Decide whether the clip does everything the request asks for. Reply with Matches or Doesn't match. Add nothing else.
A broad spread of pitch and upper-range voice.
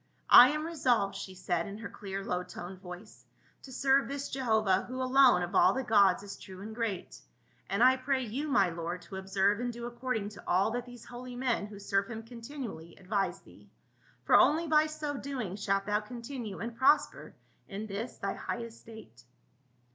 Doesn't match